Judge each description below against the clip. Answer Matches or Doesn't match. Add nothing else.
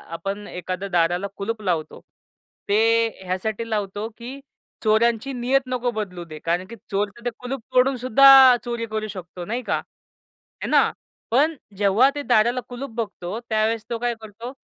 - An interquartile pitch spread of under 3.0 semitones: Doesn't match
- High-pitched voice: Matches